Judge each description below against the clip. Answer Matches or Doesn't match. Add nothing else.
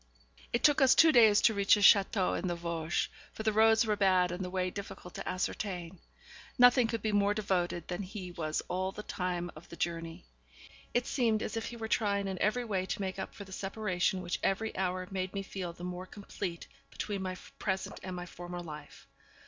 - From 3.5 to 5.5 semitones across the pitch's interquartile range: Doesn't match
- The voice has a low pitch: Doesn't match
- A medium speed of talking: Doesn't match